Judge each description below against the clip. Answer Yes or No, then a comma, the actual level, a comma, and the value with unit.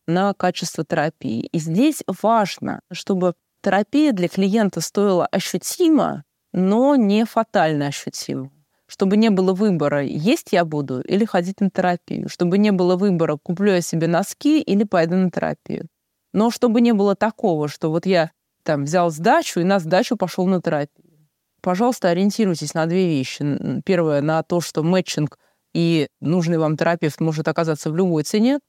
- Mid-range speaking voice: Yes, medium, 180 Hz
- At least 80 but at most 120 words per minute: No, average, 155 wpm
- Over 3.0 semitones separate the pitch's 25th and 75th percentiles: Yes, average, 4.0 semitones